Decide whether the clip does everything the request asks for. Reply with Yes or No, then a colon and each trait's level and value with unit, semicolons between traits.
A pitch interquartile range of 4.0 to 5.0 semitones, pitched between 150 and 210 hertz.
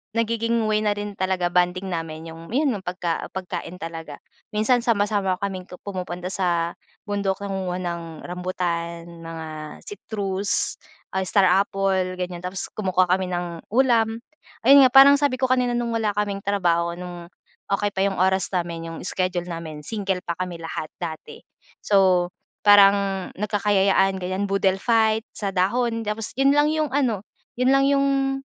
No: average, 3.4 semitones; high, 190 Hz